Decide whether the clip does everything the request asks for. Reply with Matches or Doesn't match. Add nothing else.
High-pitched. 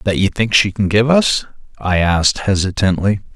Doesn't match